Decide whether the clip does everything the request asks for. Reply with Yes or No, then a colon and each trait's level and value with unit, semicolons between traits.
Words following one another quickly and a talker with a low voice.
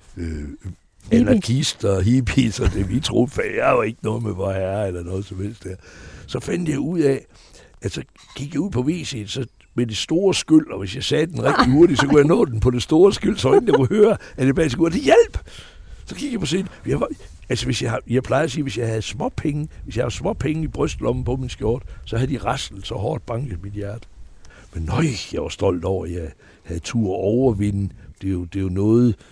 Yes: fast, 245 wpm; low, 115 Hz